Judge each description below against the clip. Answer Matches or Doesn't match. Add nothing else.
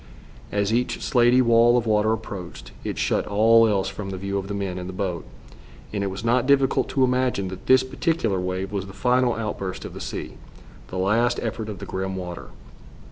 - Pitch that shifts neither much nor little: Matches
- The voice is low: Matches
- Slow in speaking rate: Doesn't match